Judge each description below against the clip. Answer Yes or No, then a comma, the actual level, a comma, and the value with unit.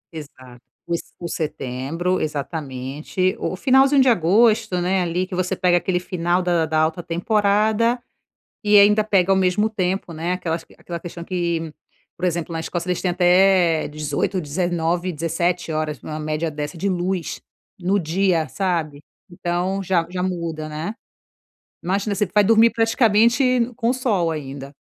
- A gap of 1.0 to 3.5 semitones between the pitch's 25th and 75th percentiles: Yes, average, 3.1 semitones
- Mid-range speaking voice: Yes, medium, 175 Hz